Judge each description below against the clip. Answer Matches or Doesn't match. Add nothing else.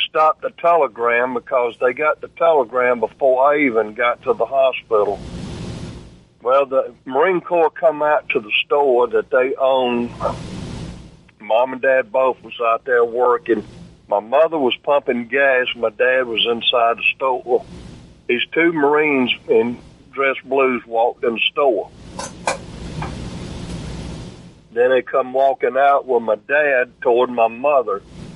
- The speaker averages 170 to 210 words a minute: Doesn't match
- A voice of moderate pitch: Doesn't match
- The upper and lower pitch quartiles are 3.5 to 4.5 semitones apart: Matches